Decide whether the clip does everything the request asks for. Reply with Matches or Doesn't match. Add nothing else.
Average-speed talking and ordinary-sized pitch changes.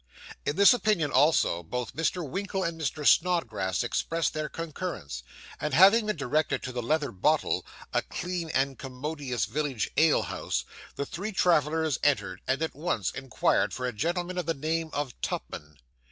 Matches